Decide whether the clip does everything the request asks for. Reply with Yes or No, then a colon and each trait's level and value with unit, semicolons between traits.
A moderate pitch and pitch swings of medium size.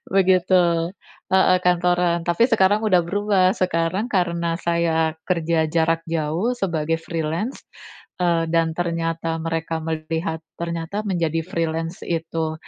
No: medium, 170 Hz; narrow, 1.9 semitones